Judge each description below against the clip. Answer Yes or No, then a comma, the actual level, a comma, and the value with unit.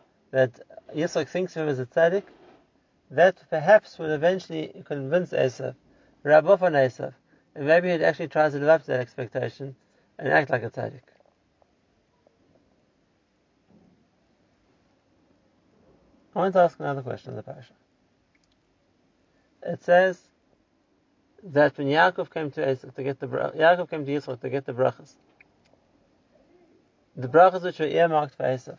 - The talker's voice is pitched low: No, medium, 155 Hz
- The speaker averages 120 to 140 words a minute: Yes, slow, 135 wpm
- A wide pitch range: No, average, 4.5 semitones